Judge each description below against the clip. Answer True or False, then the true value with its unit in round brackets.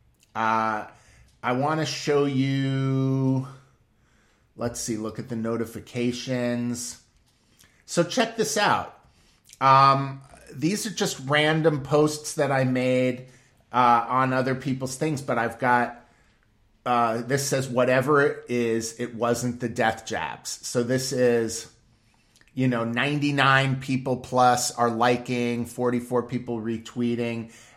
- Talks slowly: True (125 wpm)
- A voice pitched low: True (125 Hz)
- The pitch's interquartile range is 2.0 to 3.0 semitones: True (2.4 semitones)